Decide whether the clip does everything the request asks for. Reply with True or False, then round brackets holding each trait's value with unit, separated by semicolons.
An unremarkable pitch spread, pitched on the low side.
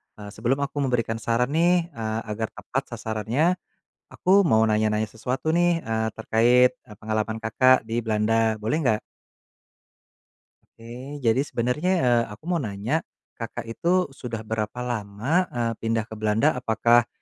True (3.6 semitones; 115 Hz)